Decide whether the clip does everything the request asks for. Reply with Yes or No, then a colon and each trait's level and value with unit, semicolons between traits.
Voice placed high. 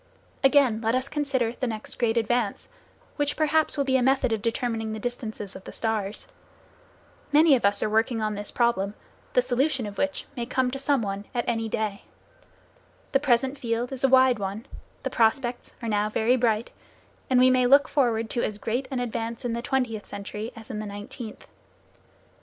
Yes: high, 235 Hz